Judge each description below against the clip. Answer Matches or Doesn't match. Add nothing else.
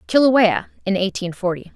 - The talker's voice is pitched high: Matches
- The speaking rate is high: Doesn't match